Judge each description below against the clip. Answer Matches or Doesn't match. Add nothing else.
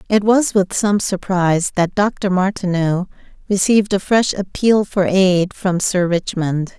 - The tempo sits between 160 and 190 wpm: Doesn't match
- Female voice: Matches